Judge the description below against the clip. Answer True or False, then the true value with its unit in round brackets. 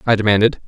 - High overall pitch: False (110 Hz)